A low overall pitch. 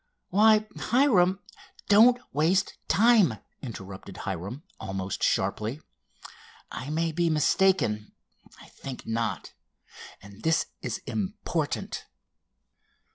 No: medium, 150 Hz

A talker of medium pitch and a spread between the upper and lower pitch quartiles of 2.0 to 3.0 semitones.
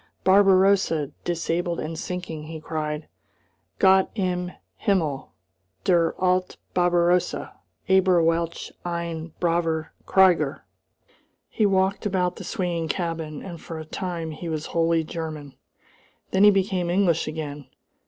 Yes: medium, 170 Hz; narrow, 2.5 semitones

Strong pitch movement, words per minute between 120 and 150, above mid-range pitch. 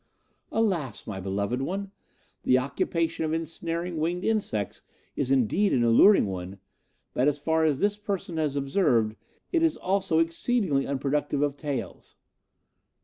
No: wide, 5.8 semitones; average, 140 wpm; medium, 155 Hz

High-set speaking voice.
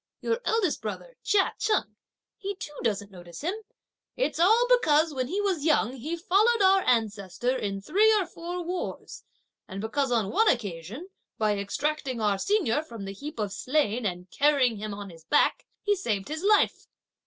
Yes: very high, 285 Hz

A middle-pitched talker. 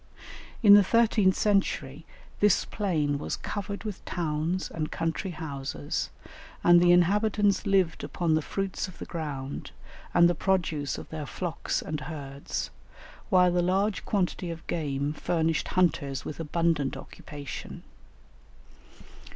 Yes: medium, 170 Hz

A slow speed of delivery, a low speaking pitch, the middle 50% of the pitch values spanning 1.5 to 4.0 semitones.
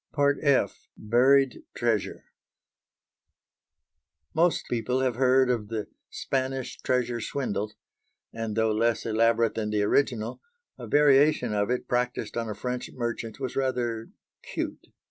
Yes: slow, 125 wpm; low, 120 Hz; average, 2.7 semitones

